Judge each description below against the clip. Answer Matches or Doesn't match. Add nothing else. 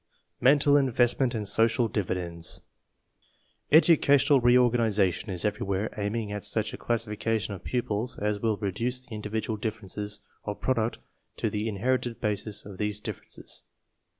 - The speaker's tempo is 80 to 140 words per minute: Matches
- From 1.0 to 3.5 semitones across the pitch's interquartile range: Matches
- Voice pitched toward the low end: Matches